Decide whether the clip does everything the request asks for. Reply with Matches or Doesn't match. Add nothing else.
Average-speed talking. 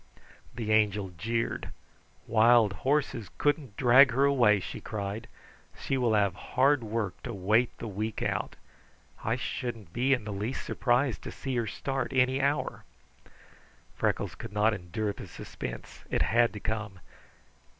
Matches